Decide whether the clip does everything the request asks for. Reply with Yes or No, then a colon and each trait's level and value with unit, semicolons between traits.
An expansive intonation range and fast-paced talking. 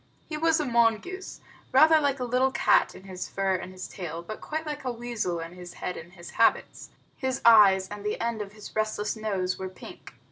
Yes: wide, 5.8 semitones; fast, 215 wpm